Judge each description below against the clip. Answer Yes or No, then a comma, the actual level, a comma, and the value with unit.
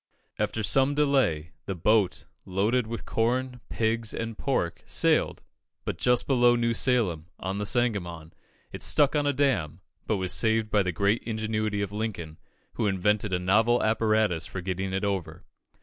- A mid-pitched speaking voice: No, low, 110 Hz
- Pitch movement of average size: Yes, average, 4.2 semitones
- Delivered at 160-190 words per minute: Yes, average, 165 wpm